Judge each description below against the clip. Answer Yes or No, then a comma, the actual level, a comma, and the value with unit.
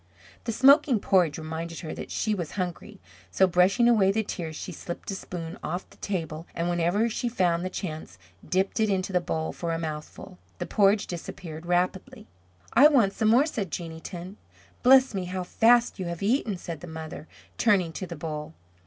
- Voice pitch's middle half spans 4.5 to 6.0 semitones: No, average, 4.0 semitones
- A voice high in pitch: No, medium, 180 Hz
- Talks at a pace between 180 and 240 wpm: Yes, average, 190 wpm